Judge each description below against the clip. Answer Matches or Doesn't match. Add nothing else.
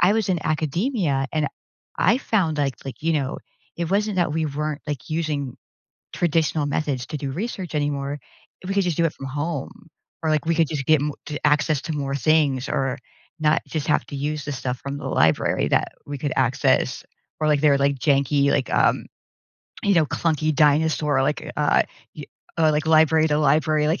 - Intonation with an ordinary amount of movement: Doesn't match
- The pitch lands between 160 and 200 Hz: Doesn't match